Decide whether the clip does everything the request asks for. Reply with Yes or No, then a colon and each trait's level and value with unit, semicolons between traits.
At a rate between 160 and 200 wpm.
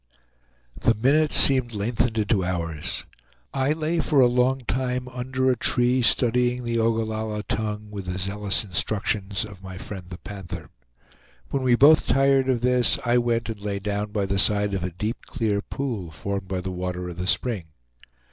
Yes: average, 180 wpm